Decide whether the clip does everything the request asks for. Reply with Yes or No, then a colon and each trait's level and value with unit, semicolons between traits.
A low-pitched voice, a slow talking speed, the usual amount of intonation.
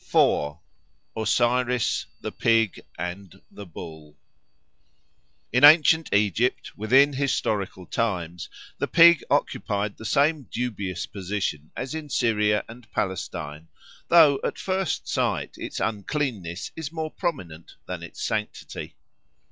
No: low, 110 Hz; slow, 115 wpm; wide, 6.7 semitones